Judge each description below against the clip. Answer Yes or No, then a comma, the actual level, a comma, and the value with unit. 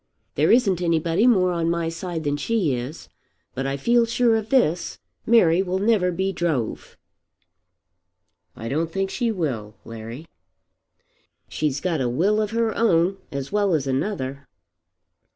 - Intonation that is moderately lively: No, wide, 6.4 semitones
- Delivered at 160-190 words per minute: No, average, 150 wpm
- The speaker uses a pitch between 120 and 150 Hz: No, medium, 170 Hz